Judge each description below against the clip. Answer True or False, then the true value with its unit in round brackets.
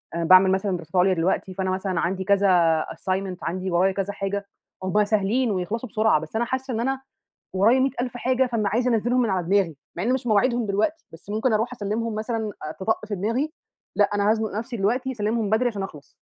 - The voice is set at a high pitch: True (210 Hz)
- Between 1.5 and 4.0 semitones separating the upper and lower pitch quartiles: True (3.7 semitones)